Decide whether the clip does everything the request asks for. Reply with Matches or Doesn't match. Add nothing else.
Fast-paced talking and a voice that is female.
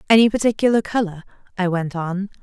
Doesn't match